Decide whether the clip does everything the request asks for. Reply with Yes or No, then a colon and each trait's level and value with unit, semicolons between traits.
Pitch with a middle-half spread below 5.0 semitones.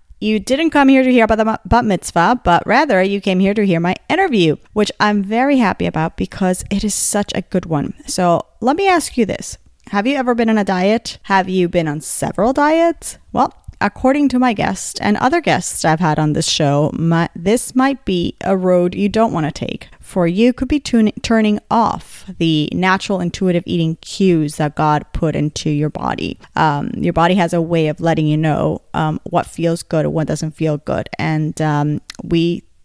No: wide, 5.6 semitones